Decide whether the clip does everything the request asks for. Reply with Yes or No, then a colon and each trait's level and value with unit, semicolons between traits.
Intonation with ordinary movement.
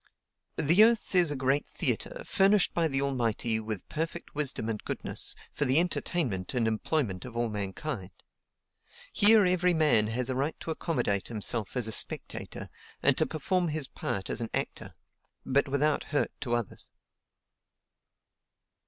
No: wide, 6.3 semitones